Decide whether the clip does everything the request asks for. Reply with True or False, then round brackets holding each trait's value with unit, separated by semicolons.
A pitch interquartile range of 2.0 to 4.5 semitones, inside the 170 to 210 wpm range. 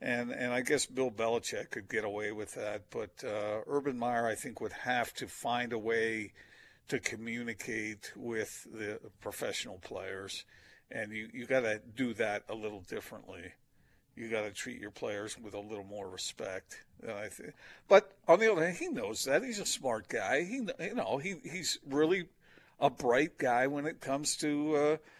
False (5.1 semitones; 180 wpm)